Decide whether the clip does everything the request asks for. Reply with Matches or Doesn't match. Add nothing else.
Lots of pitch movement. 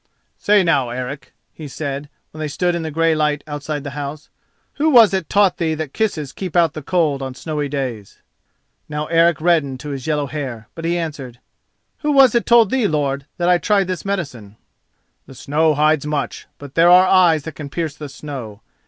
Doesn't match